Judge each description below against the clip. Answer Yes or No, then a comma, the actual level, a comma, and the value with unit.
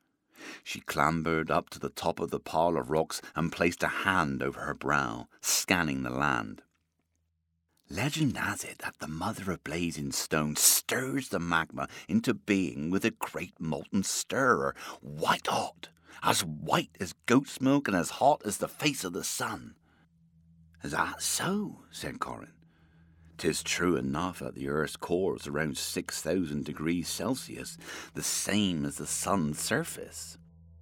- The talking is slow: No, average, 150 wpm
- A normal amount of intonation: No, narrow, 2.2 semitones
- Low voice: Yes, very low, 80 Hz